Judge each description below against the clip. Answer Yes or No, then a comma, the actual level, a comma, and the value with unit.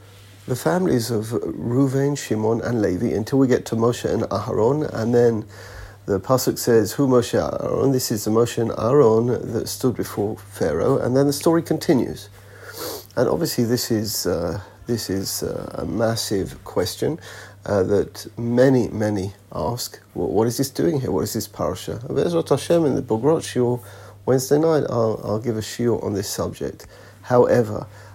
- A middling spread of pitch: Yes, average, 3.6 semitones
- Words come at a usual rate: Yes, average, 160 wpm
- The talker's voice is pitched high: No, low, 115 Hz